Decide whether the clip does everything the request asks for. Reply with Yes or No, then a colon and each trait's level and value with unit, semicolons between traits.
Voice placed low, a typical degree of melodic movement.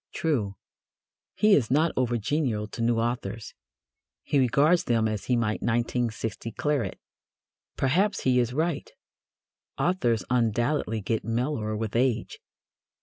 Yes: low, 120 Hz; average, 4.0 semitones